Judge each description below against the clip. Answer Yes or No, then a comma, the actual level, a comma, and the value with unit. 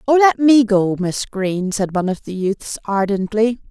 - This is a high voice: Yes, high, 210 Hz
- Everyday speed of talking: Yes, average, 195 wpm